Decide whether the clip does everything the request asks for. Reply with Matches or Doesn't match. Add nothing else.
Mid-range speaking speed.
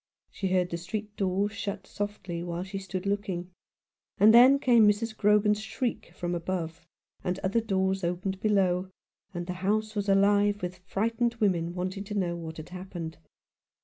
Matches